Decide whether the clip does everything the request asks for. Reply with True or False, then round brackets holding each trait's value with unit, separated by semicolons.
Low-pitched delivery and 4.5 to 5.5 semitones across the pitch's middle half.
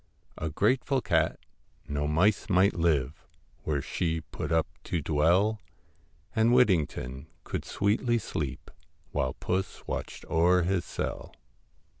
True (85 Hz; 5.1 semitones)